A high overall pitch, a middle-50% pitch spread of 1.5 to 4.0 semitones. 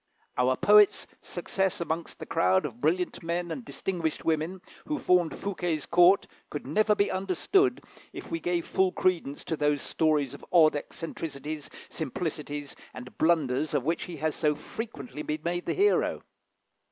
No: medium, 165 Hz; average, 3.6 semitones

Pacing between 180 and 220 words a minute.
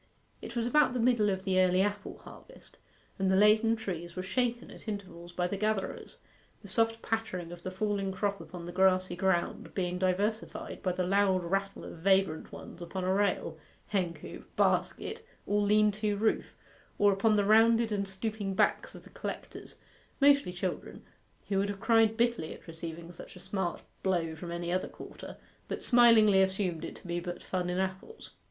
Yes: average, 185 wpm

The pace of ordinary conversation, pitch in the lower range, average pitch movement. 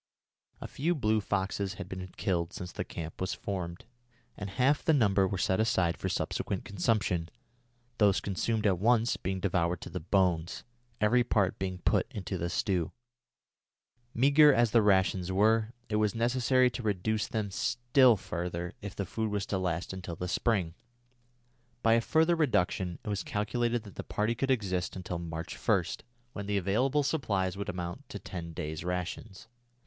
Yes: average, 170 wpm; low, 100 Hz; average, 4.0 semitones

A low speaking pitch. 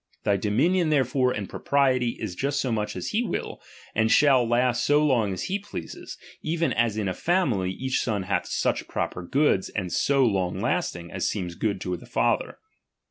Yes: low, 115 Hz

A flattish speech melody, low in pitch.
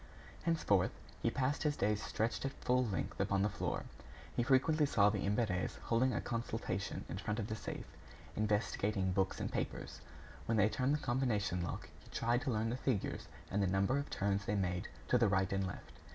No: average, 4.2 semitones; low, 105 Hz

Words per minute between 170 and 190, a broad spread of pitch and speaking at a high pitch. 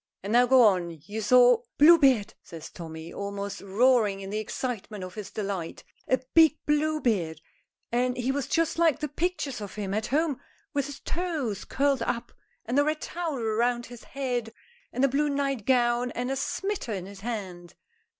Yes: average, 180 wpm; wide, 5.7 semitones; high, 245 Hz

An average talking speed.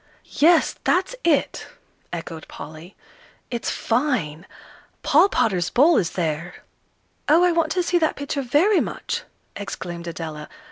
No: slow, 130 wpm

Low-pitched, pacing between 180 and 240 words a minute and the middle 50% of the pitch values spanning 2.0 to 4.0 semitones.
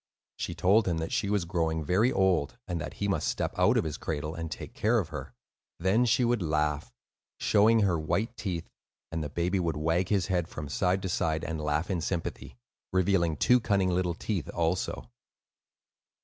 Yes: very low, 90 Hz; average, 190 wpm; average, 3.3 semitones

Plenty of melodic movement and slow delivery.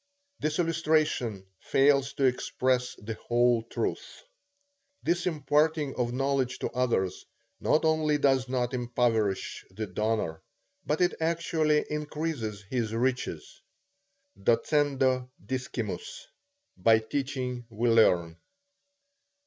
No: average, 4.6 semitones; slow, 100 wpm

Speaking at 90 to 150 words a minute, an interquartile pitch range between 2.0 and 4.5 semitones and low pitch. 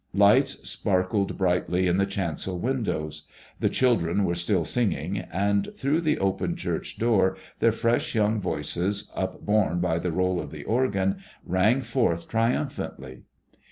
Yes: average, 140 wpm; average, 4.0 semitones; very low, 95 Hz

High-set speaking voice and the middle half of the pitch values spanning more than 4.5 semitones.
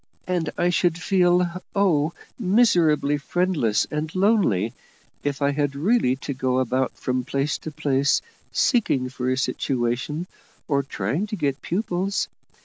No: medium, 150 Hz; wide, 5.4 semitones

